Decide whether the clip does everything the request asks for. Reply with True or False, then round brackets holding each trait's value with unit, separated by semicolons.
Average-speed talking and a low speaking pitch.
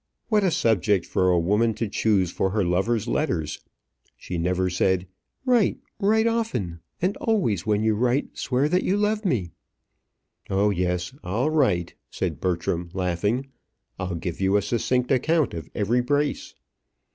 True (155 wpm; 105 Hz)